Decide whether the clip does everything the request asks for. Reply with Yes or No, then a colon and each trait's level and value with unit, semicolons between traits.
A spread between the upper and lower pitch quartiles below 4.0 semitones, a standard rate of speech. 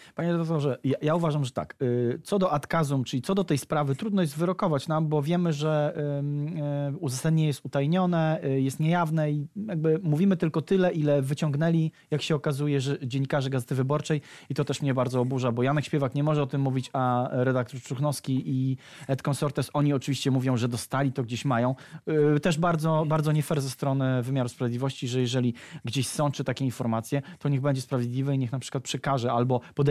No: average, 2.8 semitones; fast, 190 wpm